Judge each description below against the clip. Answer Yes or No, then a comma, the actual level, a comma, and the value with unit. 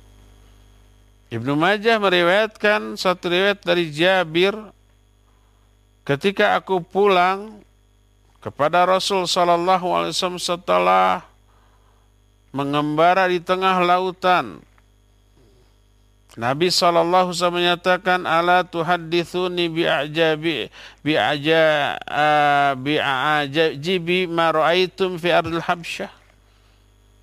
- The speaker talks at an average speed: No, slow, 80 wpm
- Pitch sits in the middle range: Yes, medium, 165 Hz